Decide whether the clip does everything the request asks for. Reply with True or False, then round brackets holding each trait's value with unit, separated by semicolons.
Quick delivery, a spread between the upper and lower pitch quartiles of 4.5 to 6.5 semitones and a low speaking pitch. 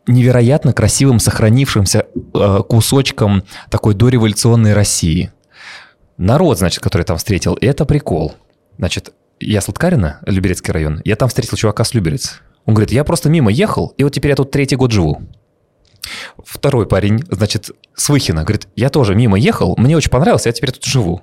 True (165 wpm; 4.9 semitones; 110 Hz)